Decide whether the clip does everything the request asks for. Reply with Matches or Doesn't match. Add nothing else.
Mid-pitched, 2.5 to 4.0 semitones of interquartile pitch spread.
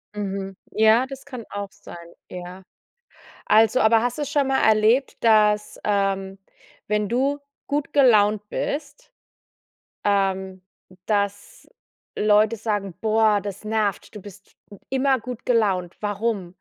Doesn't match